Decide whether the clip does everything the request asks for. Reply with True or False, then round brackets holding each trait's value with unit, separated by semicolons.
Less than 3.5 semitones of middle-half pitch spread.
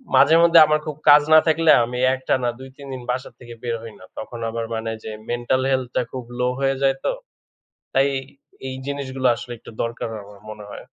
True (2.8 semitones)